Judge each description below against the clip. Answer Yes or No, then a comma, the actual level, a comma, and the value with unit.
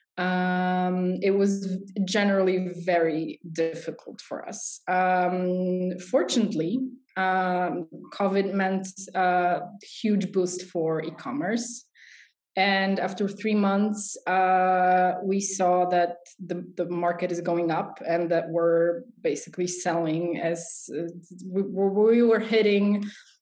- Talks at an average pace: No, slow, 110 wpm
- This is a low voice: No, medium, 185 Hz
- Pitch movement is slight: Yes, narrow, 2.1 semitones